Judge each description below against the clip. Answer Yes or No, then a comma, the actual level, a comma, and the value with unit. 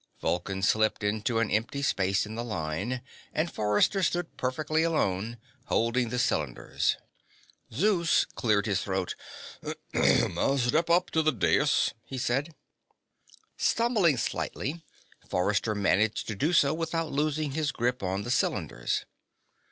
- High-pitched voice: No, low, 125 Hz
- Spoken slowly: Yes, slow, 130 wpm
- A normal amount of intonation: No, wide, 7.1 semitones